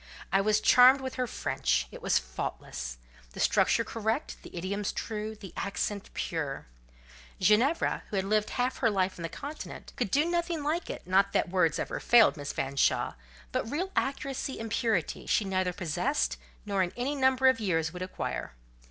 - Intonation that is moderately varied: No, wide, 6.7 semitones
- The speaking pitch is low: No, high, 205 Hz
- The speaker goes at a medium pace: Yes, average, 175 wpm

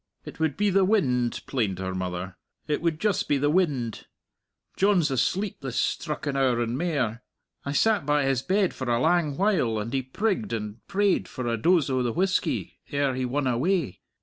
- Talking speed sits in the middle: Yes, average, 190 wpm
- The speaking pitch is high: No, medium, 140 Hz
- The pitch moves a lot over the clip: Yes, wide, 6.8 semitones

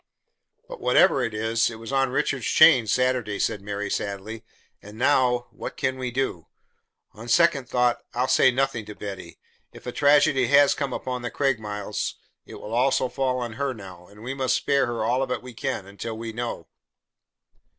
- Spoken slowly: No, average, 185 wpm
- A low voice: Yes, low, 125 Hz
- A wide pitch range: No, average, 3.3 semitones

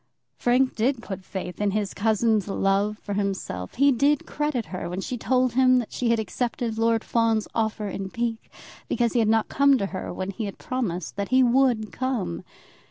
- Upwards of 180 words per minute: Yes, average, 195 wpm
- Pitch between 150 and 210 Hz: No, high, 225 Hz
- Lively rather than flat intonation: No, average, 3.9 semitones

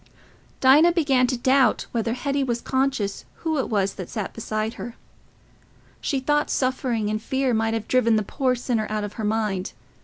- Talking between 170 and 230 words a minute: Yes, average, 180 wpm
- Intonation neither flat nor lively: Yes, average, 3.6 semitones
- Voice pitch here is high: Yes, high, 240 Hz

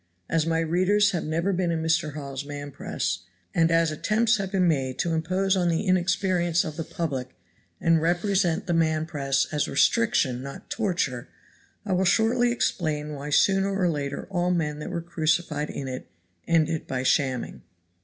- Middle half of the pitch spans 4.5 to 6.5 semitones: No, average, 3.7 semitones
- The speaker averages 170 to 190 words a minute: Yes, average, 175 wpm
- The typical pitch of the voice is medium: Yes, medium, 165 Hz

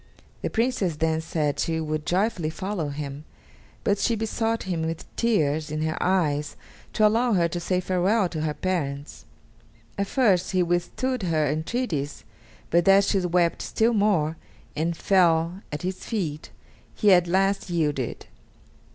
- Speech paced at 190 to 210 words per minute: No, average, 150 wpm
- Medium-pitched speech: Yes, medium, 175 Hz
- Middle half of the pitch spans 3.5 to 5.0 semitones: Yes, average, 4.2 semitones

